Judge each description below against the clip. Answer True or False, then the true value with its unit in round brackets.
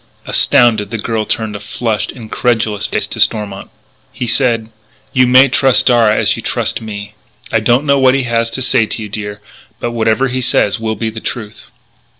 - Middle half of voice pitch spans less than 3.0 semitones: True (2.4 semitones)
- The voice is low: True (115 Hz)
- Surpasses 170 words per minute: True (190 wpm)